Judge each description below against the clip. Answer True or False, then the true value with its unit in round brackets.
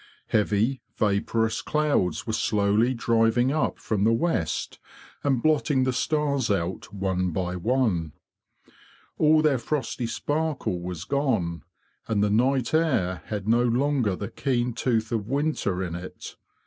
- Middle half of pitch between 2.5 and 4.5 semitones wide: False (5.4 semitones)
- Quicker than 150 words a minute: False (135 wpm)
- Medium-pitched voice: False (115 Hz)